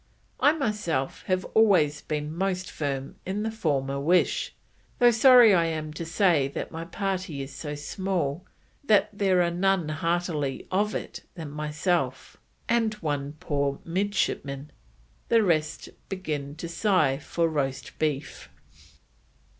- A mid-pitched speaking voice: Yes, medium, 165 Hz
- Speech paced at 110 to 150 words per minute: Yes, slow, 135 wpm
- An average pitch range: Yes, average, 4.9 semitones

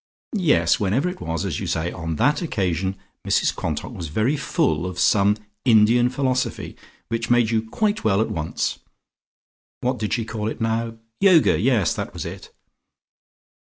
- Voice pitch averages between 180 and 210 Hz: No, low, 115 Hz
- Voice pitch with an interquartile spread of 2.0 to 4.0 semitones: No, average, 4.9 semitones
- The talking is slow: No, average, 160 wpm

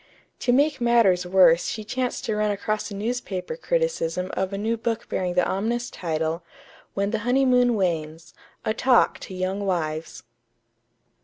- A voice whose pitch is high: Yes, high, 205 Hz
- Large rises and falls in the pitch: No, average, 4.8 semitones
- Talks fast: No, average, 155 wpm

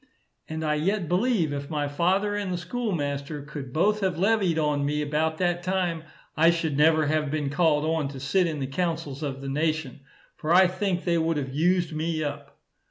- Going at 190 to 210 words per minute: Yes, average, 200 wpm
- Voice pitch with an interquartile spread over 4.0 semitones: No, average, 3.2 semitones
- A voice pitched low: No, medium, 160 Hz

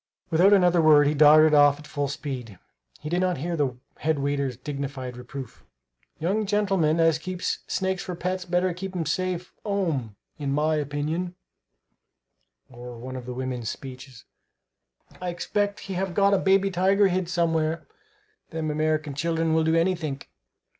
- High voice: No, medium, 160 Hz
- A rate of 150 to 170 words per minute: Yes, average, 160 wpm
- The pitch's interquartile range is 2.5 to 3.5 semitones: No, average, 4.4 semitones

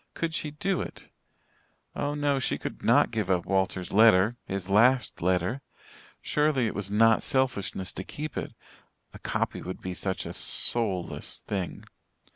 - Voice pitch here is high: No, low, 110 Hz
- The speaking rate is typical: Yes, average, 155 wpm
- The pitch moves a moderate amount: No, wide, 6.1 semitones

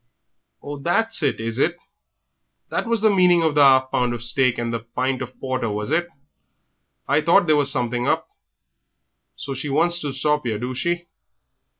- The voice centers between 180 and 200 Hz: No, medium, 140 Hz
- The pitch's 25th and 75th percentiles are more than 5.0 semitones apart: Yes, wide, 5.5 semitones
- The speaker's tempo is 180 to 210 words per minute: Yes, average, 185 wpm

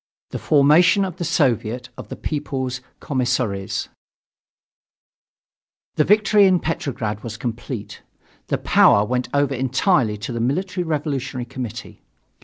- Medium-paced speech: No, slow, 120 wpm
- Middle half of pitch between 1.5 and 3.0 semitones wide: No, average, 4.7 semitones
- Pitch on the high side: No, low, 130 Hz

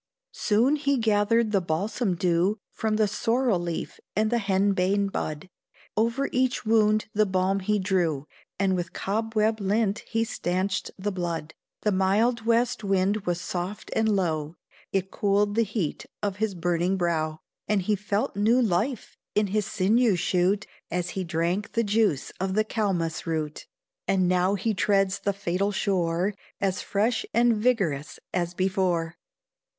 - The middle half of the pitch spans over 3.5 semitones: No, average, 3.2 semitones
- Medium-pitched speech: No, high, 200 Hz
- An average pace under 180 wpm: Yes, average, 155 wpm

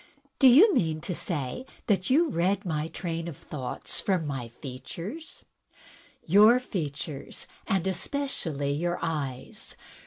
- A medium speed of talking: No, slow, 130 wpm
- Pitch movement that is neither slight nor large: No, wide, 5.7 semitones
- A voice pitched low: No, medium, 170 Hz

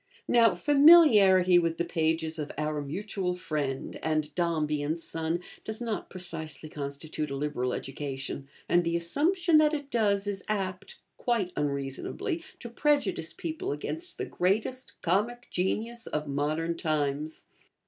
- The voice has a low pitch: No, medium, 175 Hz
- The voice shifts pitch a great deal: Yes, wide, 6.3 semitones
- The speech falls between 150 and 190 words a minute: No, slow, 135 wpm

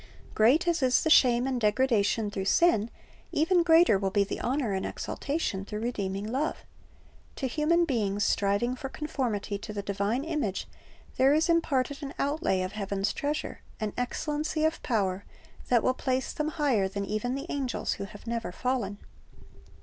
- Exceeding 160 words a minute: Yes, average, 170 wpm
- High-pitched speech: Yes, high, 245 Hz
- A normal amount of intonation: No, wide, 6.3 semitones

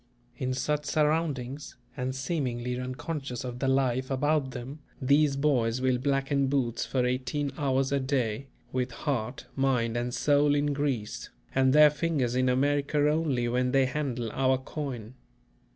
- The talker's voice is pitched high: No, low, 130 Hz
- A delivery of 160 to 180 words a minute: No, average, 150 wpm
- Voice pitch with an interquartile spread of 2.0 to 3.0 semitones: Yes, narrow, 2.5 semitones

